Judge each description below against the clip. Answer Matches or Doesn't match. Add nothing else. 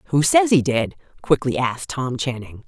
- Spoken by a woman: Matches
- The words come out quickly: Doesn't match